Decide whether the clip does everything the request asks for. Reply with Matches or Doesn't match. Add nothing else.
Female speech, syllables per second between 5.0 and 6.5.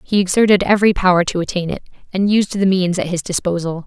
Matches